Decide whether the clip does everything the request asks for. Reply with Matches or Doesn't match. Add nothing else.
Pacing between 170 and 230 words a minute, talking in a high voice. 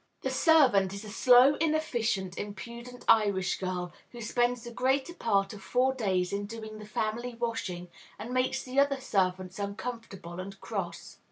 Doesn't match